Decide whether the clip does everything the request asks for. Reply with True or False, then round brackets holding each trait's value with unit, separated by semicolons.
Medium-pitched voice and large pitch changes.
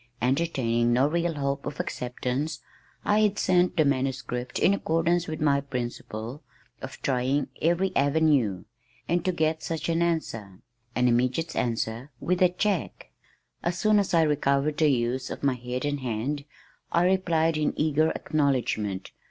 False (145 Hz; 4.8 semitones)